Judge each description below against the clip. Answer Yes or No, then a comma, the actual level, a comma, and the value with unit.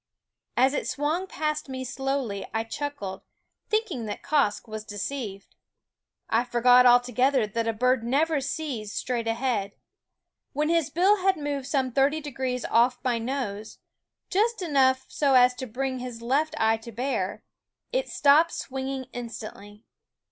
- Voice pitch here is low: No, very high, 255 Hz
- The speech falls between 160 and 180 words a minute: No, average, 145 wpm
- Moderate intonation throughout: Yes, average, 4.0 semitones